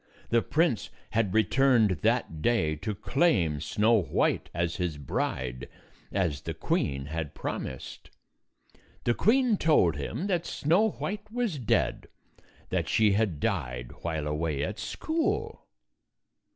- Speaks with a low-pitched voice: Yes, low, 105 Hz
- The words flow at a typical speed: No, slow, 125 wpm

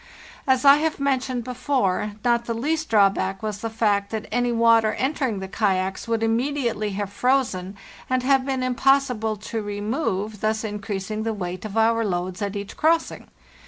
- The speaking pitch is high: Yes, high, 225 Hz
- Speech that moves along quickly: No, average, 170 wpm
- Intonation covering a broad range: No, average, 3.9 semitones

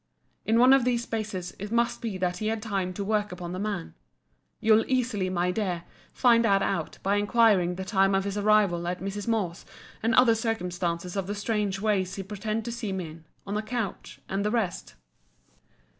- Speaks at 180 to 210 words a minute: Yes, average, 200 wpm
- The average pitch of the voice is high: Yes, high, 205 Hz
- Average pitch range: Yes, average, 3.2 semitones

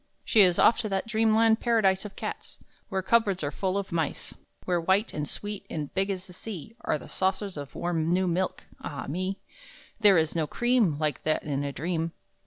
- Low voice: No, medium, 185 Hz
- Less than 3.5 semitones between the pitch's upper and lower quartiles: No, average, 4.3 semitones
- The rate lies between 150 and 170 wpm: No, fast, 205 wpm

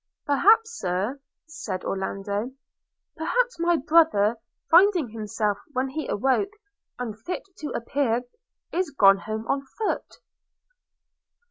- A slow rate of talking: Yes, slow, 110 wpm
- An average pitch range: No, wide, 7.8 semitones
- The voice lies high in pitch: Yes, very high, 270 Hz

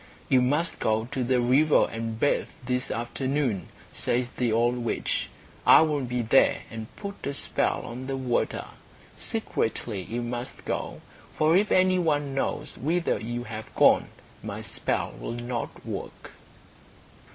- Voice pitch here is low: Yes, low, 125 Hz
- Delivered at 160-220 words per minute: No, average, 150 wpm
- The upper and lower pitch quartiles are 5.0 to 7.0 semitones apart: No, average, 3.6 semitones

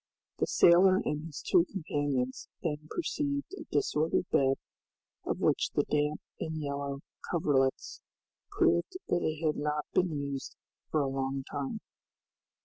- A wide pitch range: No, average, 3.5 semitones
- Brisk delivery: No, average, 140 wpm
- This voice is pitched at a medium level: Yes, medium, 150 Hz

